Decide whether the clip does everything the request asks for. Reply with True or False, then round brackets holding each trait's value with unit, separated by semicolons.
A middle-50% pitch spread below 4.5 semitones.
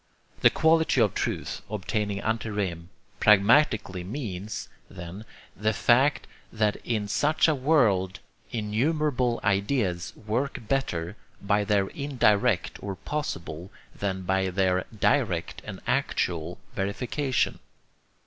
False (4.9 semitones)